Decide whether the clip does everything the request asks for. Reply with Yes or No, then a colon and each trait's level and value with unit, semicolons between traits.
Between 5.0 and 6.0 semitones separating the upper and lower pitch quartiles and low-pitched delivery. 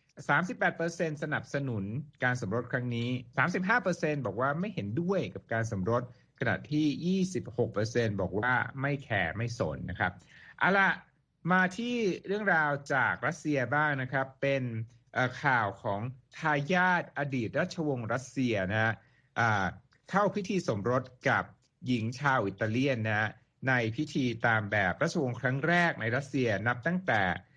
No: average, 4.5 semitones; low, 130 Hz